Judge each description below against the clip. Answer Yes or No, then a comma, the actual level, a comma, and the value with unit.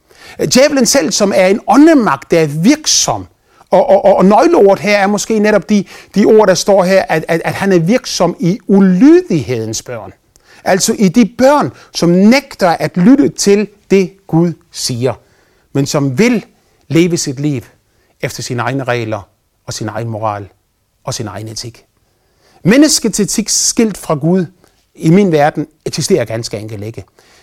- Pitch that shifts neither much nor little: No, wide, 8.1 semitones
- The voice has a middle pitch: Yes, medium, 180 Hz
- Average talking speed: Yes, average, 160 wpm